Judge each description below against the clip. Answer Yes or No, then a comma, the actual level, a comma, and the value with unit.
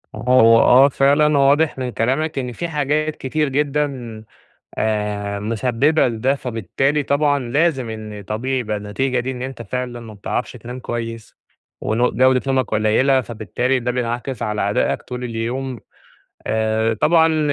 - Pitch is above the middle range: No, low, 125 Hz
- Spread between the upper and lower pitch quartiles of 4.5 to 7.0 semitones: No, average, 3.4 semitones